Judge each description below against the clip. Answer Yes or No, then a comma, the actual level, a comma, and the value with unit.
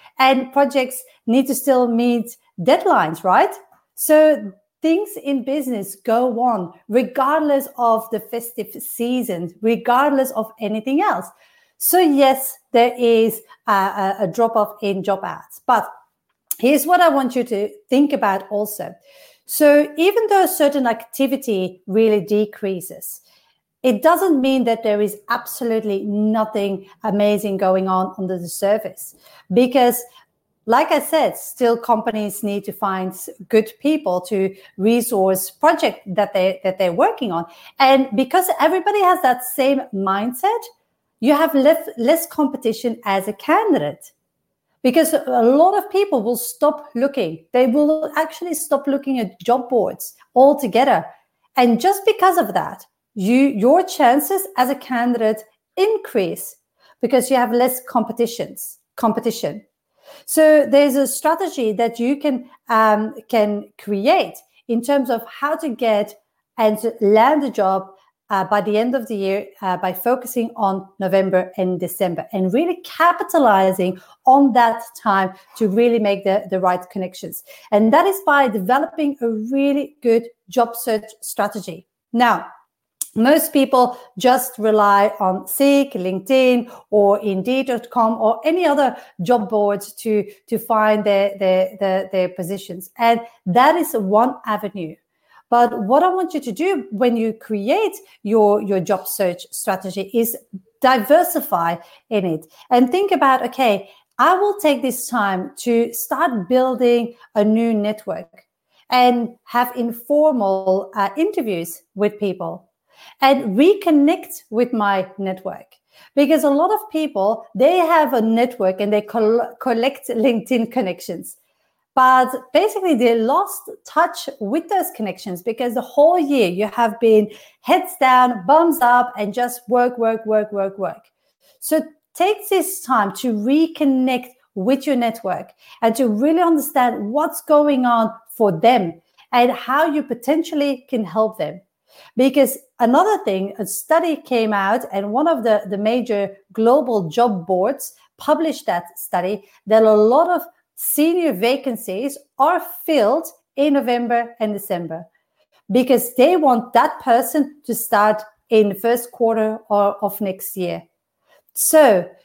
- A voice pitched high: Yes, high, 240 Hz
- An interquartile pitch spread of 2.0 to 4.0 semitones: No, average, 5.2 semitones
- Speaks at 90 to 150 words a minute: Yes, average, 140 wpm